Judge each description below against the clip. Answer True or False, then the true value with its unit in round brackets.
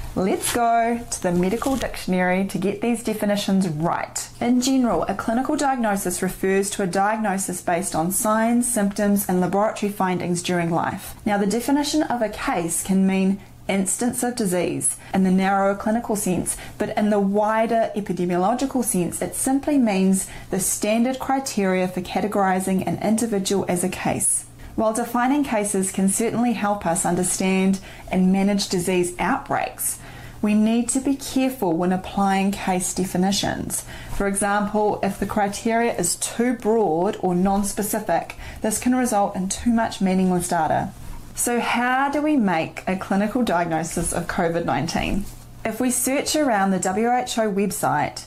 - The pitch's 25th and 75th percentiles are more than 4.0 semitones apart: False (3.6 semitones)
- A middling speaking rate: True (150 wpm)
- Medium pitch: False (200 Hz)